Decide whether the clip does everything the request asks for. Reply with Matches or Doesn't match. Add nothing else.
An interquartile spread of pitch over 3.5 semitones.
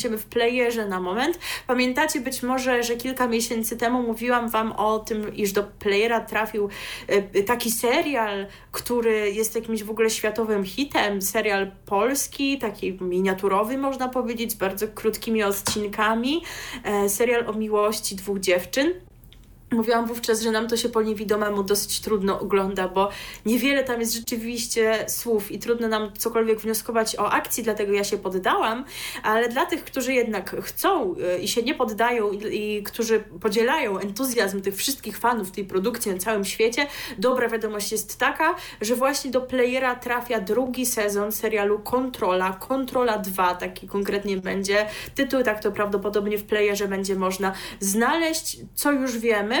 Doesn't match